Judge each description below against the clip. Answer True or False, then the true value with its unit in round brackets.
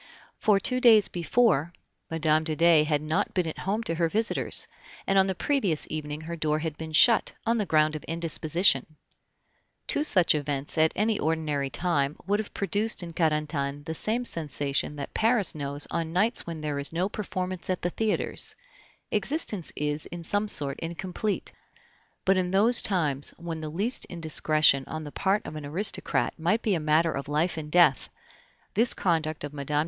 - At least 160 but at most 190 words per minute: True (180 wpm)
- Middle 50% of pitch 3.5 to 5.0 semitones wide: True (4.2 semitones)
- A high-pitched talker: False (165 Hz)